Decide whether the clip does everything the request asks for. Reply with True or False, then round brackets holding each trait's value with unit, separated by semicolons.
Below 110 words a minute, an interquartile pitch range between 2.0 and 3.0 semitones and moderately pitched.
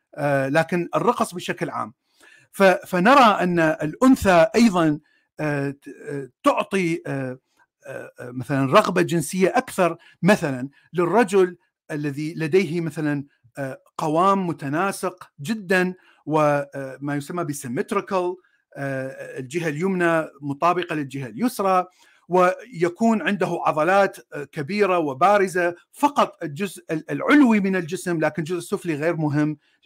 False (90 wpm; 4.1 semitones; 175 Hz)